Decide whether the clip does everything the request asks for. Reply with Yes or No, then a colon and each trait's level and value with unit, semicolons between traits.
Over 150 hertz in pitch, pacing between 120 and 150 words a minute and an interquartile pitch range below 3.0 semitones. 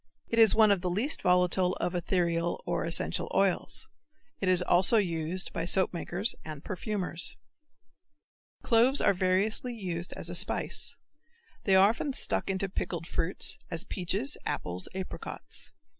Yes: medium, 185 Hz; average, 145 wpm; narrow, 2.6 semitones